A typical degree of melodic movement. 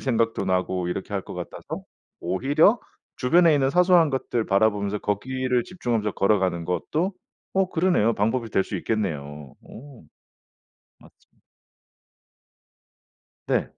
No: wide, 6.7 semitones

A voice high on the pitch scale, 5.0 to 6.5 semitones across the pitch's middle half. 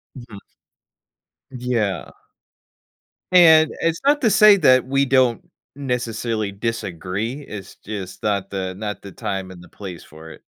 No: low, 110 Hz; wide, 5.4 semitones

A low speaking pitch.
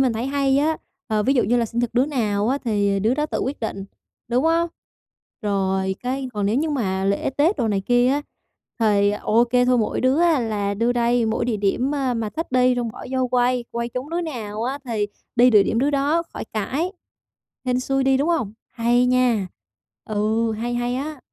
No: high, 245 Hz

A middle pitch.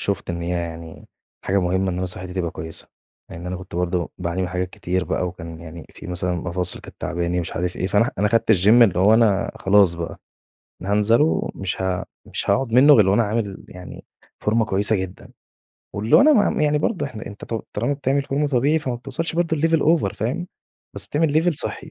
No: very low, 95 Hz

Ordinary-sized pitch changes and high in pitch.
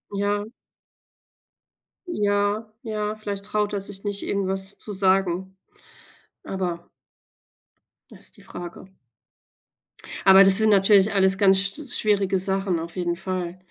No: narrow, 1.4 semitones; high, 195 Hz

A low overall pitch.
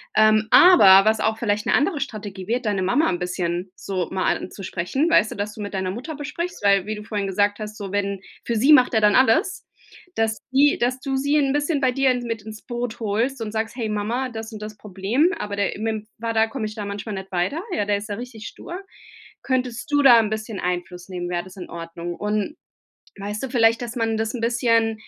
No: high, 220 Hz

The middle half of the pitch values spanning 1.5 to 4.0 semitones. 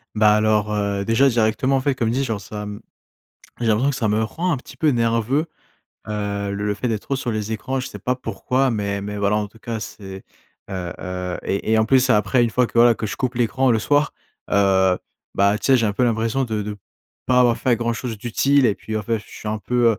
Yes: average, 3.2 semitones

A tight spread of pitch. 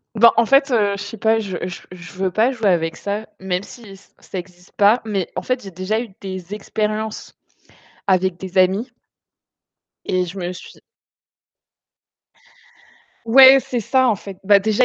No: average, 3.2 semitones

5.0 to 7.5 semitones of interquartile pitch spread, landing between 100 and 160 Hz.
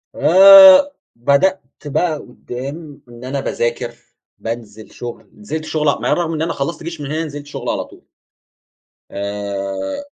Yes: wide, 5.6 semitones; medium, 140 Hz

